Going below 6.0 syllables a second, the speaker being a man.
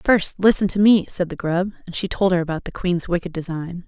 No: 5.6 syllables/s; female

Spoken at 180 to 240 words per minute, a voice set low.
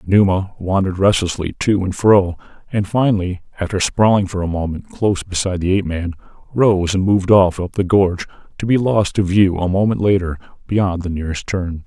Yes: average, 185 wpm; very low, 95 Hz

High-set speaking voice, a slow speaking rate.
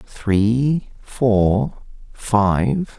No: low, 115 Hz; slow, 60 wpm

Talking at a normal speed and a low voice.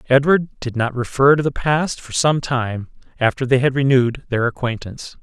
Yes: average, 185 wpm; low, 130 Hz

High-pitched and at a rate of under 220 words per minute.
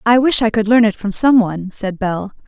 No: high, 215 Hz; fast, 265 wpm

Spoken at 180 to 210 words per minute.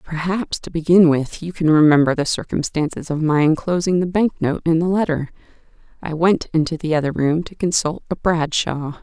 Yes: average, 185 wpm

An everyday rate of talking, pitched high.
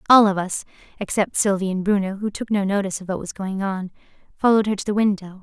No: fast, 230 wpm; high, 195 Hz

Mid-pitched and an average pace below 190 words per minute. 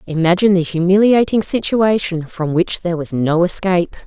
Yes: medium, 180 Hz; average, 150 wpm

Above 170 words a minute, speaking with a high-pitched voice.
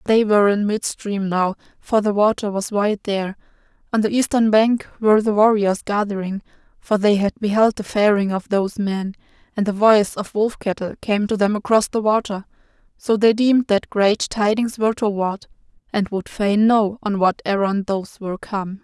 Yes: average, 185 wpm; high, 205 Hz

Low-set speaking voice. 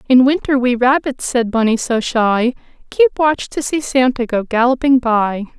No: very high, 250 Hz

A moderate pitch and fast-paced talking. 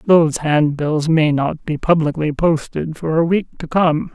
No: medium, 160 Hz; average, 175 wpm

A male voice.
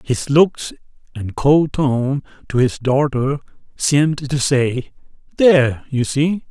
Yes: male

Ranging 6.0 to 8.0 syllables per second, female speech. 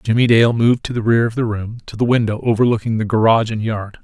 No: 6.4 syllables/s; male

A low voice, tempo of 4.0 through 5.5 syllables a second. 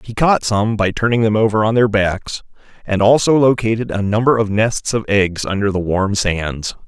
Yes: low, 105 Hz; 4.8 syllables/s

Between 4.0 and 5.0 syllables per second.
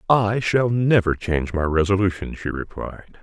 Yes: 4.9 syllables/s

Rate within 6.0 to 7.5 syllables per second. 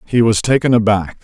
Yes: 6.1 syllables/s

